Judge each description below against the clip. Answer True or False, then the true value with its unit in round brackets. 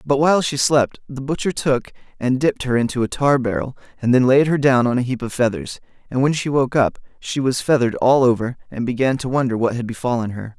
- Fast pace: True (240 wpm)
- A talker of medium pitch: False (125 Hz)